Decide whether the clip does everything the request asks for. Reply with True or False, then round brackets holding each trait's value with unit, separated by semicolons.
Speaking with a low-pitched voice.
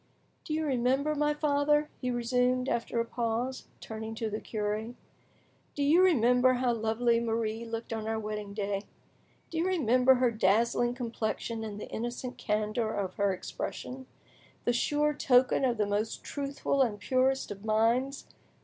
False (235 Hz)